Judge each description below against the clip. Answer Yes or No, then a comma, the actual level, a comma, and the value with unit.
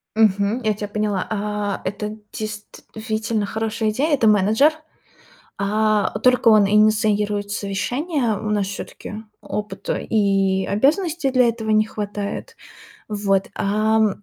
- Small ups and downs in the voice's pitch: Yes, narrow, 1.5 semitones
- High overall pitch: Yes, high, 215 Hz